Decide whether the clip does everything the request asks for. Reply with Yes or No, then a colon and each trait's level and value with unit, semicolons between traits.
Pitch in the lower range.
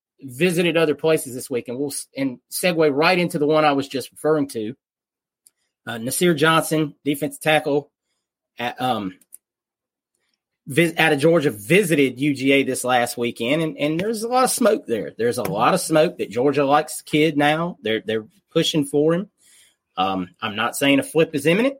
No: medium, 150 Hz